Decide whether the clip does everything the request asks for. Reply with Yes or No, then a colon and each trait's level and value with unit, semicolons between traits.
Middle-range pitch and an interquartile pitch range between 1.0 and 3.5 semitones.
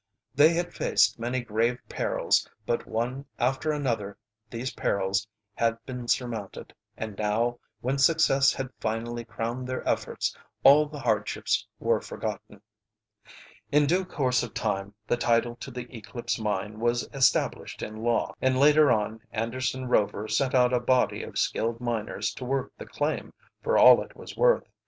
No: low, 120 Hz; average, 2.9 semitones